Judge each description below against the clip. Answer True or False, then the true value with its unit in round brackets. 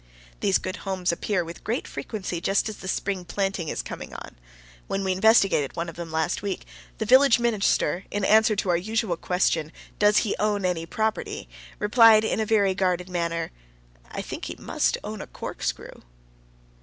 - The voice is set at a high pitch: True (195 Hz)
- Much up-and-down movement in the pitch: False (3.5 semitones)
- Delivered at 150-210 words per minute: True (180 wpm)